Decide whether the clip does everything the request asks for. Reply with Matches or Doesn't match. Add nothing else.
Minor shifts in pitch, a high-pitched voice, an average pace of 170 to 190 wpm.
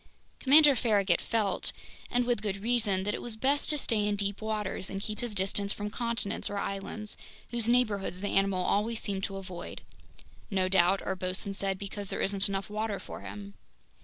Matches